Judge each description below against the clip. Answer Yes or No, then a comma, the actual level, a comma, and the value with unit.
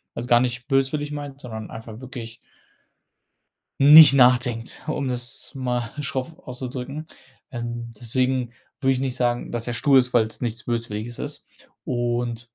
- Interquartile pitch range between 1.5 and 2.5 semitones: Yes, narrow, 2.0 semitones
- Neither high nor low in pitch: No, low, 125 Hz